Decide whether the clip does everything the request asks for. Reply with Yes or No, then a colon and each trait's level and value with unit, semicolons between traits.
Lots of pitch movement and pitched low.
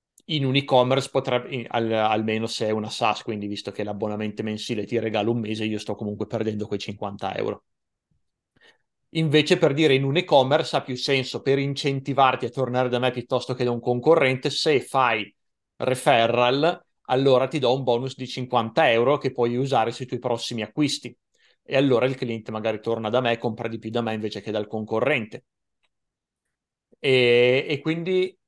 No: average, 3.4 semitones; low, 125 Hz